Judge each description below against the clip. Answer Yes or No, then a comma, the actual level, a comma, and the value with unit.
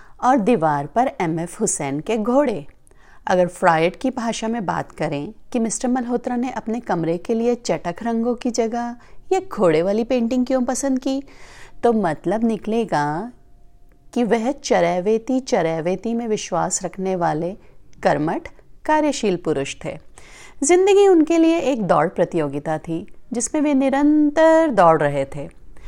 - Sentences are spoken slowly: No, average, 145 wpm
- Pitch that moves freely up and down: Yes, wide, 7.1 semitones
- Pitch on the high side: Yes, high, 225 Hz